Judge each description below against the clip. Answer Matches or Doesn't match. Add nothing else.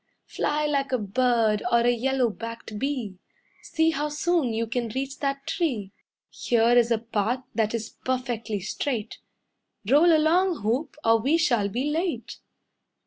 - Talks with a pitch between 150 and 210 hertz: Doesn't match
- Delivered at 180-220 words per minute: Doesn't match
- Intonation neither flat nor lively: Matches